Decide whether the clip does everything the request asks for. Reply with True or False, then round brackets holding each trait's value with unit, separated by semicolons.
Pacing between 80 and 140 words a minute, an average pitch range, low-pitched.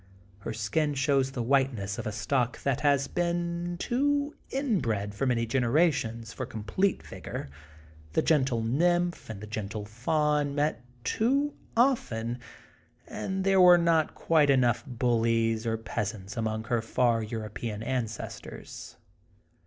False (135 wpm; 6.5 semitones; 130 Hz)